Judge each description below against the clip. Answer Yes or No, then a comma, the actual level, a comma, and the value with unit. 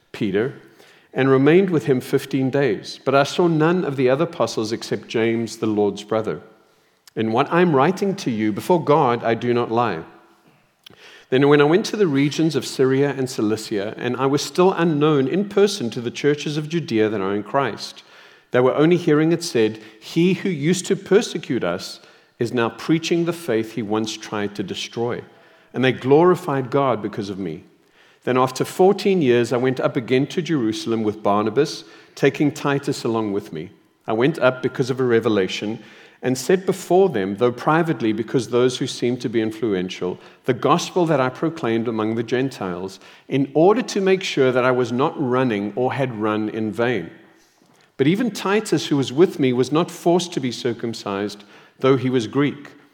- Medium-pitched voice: No, low, 130 Hz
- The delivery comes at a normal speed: Yes, average, 190 wpm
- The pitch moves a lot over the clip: Yes, wide, 5.8 semitones